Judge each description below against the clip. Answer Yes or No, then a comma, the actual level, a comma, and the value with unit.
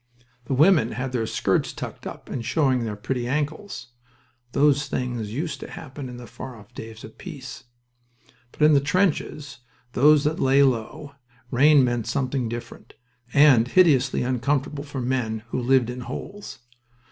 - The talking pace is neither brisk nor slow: Yes, average, 160 wpm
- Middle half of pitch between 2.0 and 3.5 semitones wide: Yes, average, 3.2 semitones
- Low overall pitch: Yes, low, 130 Hz